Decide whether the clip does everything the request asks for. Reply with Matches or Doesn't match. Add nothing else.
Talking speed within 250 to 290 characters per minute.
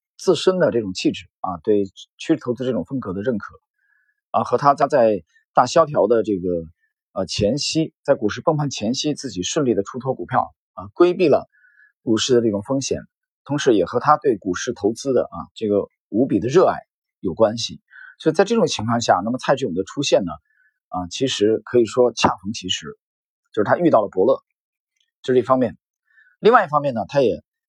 Matches